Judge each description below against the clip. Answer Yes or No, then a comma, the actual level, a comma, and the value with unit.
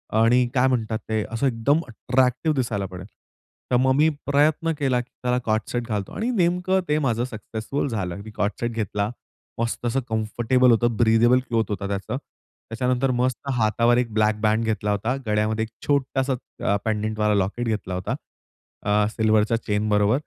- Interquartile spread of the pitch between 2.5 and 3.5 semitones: Yes, average, 2.9 semitones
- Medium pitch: No, low, 115 Hz